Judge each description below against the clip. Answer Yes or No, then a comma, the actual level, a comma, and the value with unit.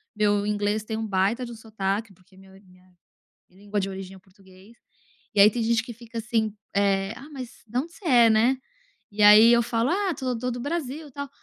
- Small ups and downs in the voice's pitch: No, average, 3.4 semitones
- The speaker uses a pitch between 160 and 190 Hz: No, high, 220 Hz